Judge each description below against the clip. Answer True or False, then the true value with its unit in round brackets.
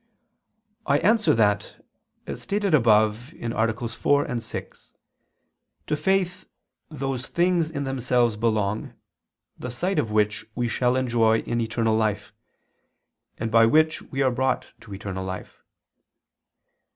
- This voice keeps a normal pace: False (125 wpm)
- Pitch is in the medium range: False (120 Hz)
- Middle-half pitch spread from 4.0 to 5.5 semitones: True (4.3 semitones)